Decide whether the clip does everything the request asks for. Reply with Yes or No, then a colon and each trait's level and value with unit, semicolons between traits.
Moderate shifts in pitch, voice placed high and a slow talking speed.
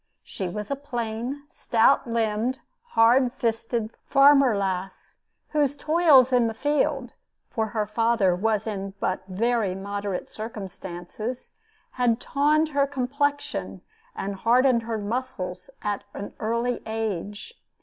Yes: average, 4.1 semitones; high, 230 Hz; slow, 120 wpm